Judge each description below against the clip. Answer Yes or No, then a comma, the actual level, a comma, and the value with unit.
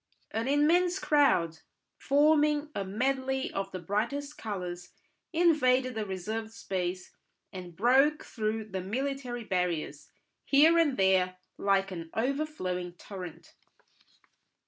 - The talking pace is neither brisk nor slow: No, slow, 110 wpm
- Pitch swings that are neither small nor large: No, wide, 7.3 semitones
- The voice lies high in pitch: Yes, high, 220 Hz